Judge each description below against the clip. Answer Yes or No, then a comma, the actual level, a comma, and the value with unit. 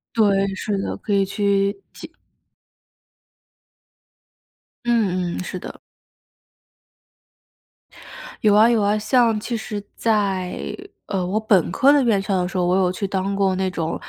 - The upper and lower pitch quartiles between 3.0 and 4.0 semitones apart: No, narrow, 2.4 semitones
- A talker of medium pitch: No, high, 200 Hz